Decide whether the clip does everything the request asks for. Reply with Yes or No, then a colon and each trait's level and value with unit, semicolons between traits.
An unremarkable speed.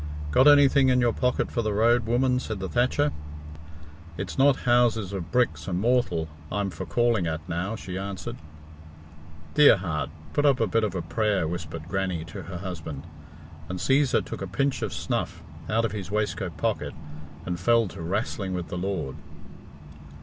Yes: average, 175 wpm